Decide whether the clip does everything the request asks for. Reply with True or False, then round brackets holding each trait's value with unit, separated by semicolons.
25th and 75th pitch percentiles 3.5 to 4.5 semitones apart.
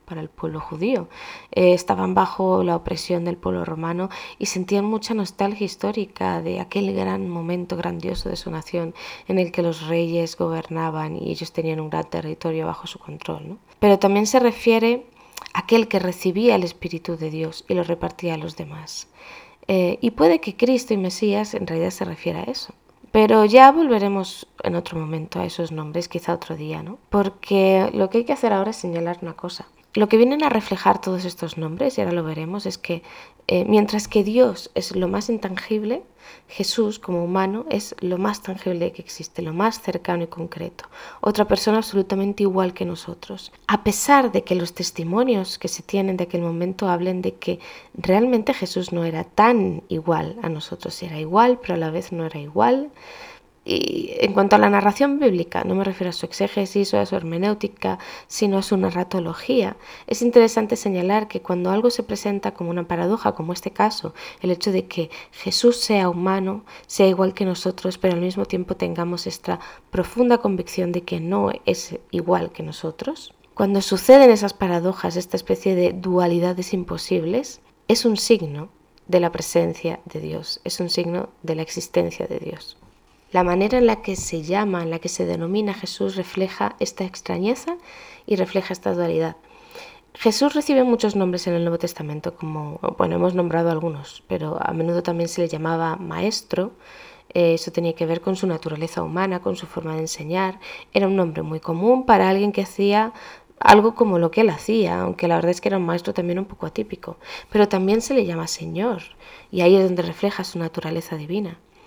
True (3.8 semitones)